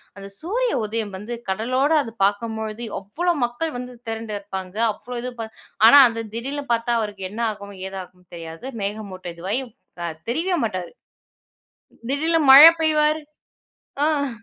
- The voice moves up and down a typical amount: No, wide, 5.9 semitones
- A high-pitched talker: Yes, high, 230 Hz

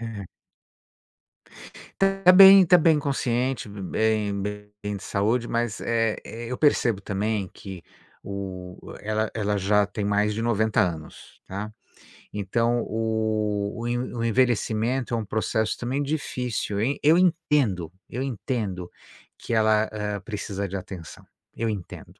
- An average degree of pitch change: Yes, average, 3.1 semitones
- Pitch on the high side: No, low, 110 Hz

